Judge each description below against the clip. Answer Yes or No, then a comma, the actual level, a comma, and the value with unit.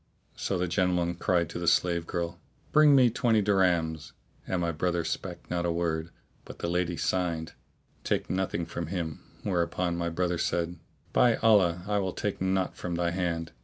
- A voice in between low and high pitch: No, very low, 85 Hz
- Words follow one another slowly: No, average, 180 wpm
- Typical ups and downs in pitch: No, narrow, 1.7 semitones